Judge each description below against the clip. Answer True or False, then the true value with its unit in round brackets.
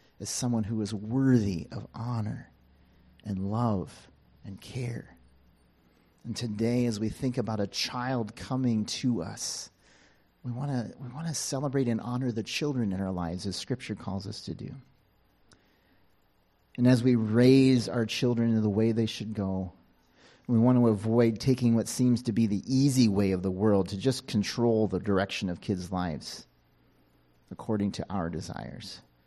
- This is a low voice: True (110 Hz)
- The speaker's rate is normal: True (160 wpm)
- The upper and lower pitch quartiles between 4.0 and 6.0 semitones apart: True (4.3 semitones)